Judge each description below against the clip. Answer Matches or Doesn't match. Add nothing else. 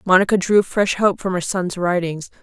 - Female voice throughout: Matches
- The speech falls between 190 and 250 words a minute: Matches